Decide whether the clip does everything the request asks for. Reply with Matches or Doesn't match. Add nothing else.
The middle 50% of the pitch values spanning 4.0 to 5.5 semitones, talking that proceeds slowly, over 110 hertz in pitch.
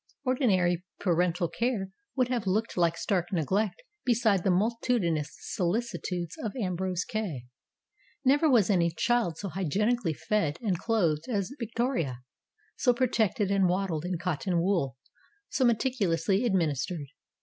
Matches